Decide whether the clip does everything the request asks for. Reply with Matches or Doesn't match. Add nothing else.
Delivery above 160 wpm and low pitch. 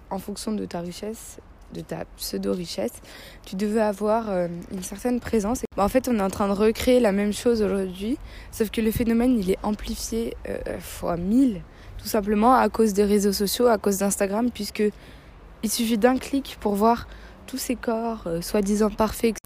Doesn't match